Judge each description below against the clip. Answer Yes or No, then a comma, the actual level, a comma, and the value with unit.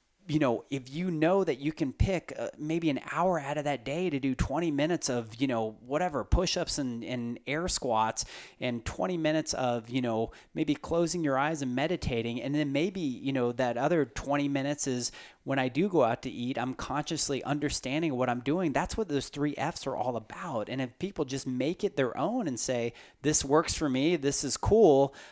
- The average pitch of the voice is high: No, medium, 140 Hz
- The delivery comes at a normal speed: No, fast, 215 wpm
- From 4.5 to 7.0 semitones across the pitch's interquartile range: No, average, 3.7 semitones